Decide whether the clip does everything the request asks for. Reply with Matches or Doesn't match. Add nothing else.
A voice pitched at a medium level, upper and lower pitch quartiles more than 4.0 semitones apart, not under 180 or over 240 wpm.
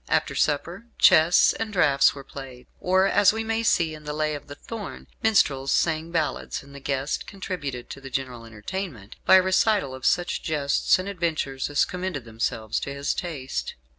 Matches